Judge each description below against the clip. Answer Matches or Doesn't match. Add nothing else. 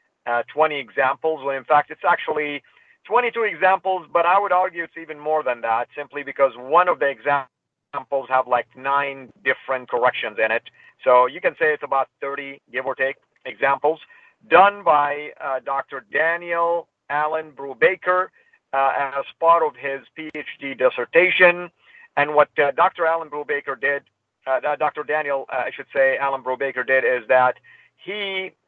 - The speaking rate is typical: Matches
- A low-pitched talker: Doesn't match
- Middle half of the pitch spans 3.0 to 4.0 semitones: Matches